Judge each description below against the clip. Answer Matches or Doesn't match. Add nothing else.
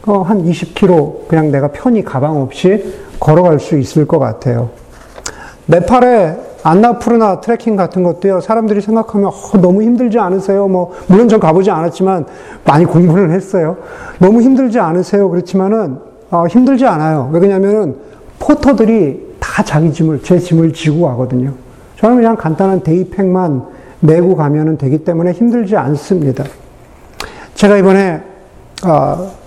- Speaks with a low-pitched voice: Doesn't match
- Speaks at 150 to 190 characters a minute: Doesn't match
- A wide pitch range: Doesn't match